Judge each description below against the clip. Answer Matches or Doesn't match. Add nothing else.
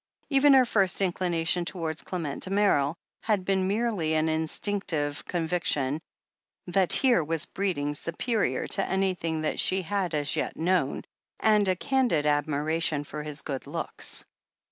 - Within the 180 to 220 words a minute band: Doesn't match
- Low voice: Doesn't match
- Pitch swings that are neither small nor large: Matches